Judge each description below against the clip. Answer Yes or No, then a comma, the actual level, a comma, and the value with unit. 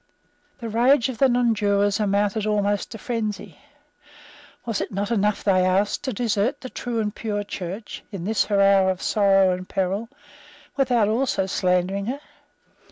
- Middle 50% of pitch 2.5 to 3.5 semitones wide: Yes, average, 2.8 semitones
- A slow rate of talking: No, average, 160 wpm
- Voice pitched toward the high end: Yes, high, 205 Hz